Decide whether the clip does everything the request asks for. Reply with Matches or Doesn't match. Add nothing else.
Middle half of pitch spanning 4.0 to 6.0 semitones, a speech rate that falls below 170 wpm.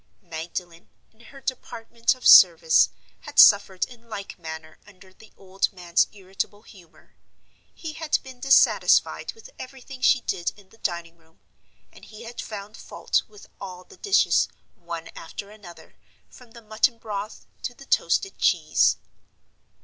Matches